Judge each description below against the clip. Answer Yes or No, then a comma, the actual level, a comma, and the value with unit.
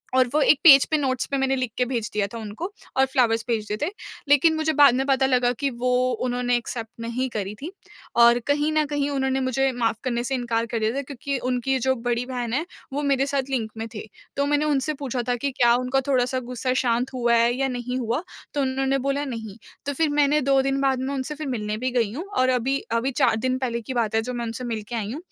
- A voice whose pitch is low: No, very high, 255 Hz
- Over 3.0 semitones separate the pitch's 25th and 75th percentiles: No, narrow, 2.5 semitones